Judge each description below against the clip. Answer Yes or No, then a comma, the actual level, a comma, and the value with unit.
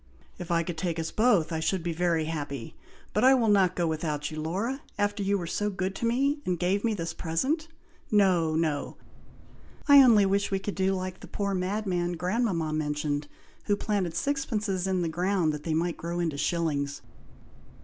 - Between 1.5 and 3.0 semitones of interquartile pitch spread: No, average, 4.0 semitones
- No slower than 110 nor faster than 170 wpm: No, average, 200 wpm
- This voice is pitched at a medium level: Yes, medium, 180 Hz